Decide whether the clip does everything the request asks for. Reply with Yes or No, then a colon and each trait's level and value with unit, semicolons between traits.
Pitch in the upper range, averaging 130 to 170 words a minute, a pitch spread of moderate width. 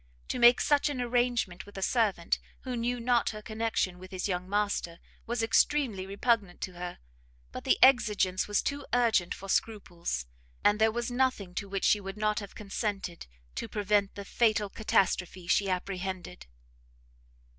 Yes: high, 205 Hz; average, 165 wpm; average, 3.8 semitones